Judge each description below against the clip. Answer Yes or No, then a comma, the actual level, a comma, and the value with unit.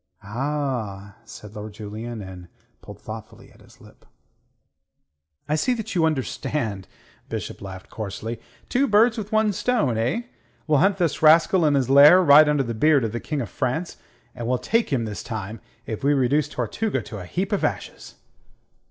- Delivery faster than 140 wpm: Yes, average, 180 wpm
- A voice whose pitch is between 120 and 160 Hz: Yes, low, 135 Hz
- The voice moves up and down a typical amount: No, wide, 7.0 semitones